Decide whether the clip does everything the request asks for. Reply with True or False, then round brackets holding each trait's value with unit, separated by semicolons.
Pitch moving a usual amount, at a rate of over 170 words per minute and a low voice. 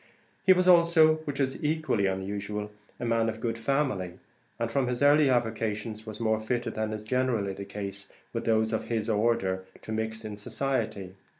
True (3.7 semitones; 180 wpm; 110 Hz)